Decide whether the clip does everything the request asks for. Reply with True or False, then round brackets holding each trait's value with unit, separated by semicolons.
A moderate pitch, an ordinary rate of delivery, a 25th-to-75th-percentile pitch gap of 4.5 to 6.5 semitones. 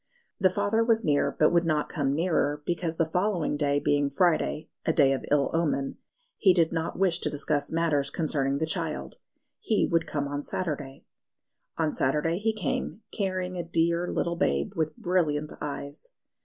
False (160 Hz; 170 wpm; 3.4 semitones)